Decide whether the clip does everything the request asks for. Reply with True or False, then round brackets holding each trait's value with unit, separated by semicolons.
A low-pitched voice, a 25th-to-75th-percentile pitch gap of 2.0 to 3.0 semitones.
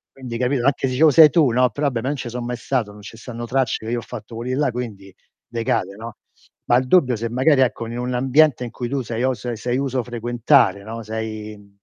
True (120 Hz; 2.4 semitones)